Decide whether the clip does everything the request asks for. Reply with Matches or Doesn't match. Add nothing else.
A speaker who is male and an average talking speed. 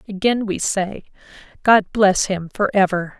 Doesn't match